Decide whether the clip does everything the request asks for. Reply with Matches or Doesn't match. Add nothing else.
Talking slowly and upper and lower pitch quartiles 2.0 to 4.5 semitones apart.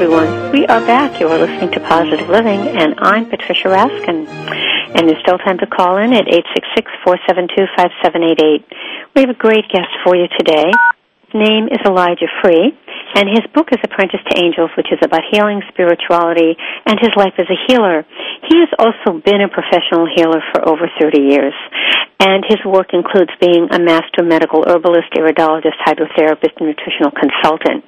Doesn't match